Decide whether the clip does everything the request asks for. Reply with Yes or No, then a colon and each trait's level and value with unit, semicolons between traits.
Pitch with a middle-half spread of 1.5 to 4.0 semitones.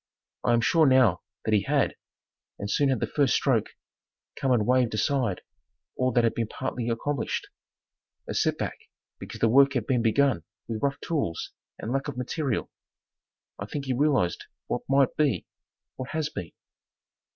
Yes: average, 3.6 semitones